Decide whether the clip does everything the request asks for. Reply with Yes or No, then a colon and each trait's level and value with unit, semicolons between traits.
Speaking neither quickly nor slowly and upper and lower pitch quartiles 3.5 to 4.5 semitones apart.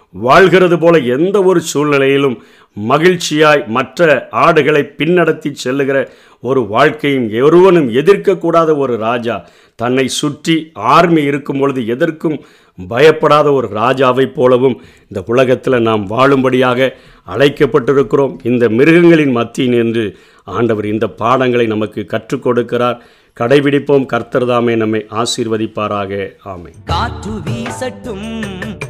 Yes: average, 100 wpm; average, 4.2 semitones